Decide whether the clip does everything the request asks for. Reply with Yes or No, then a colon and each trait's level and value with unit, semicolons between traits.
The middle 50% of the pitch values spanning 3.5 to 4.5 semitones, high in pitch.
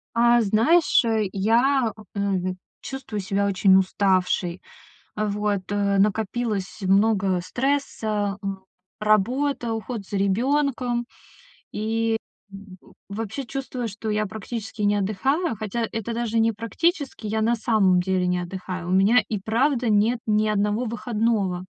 No: average, 3.1 semitones; high, 215 Hz